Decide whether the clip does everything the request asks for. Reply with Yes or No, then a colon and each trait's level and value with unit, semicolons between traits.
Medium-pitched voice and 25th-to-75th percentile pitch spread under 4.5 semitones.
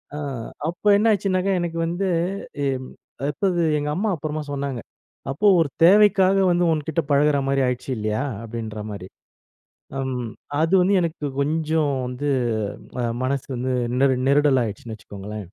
No: medium, 145 Hz; average, 5.0 semitones